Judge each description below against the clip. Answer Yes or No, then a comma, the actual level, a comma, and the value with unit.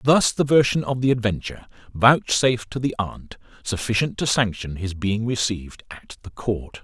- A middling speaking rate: Yes, average, 160 wpm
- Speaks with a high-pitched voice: No, low, 115 Hz